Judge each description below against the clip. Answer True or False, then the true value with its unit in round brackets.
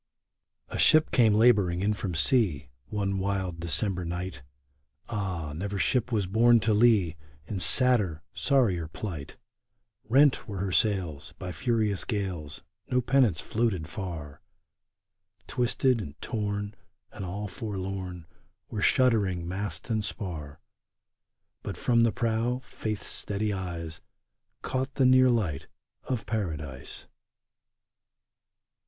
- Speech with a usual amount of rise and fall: True (4.8 semitones)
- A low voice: True (100 Hz)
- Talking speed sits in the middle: False (120 wpm)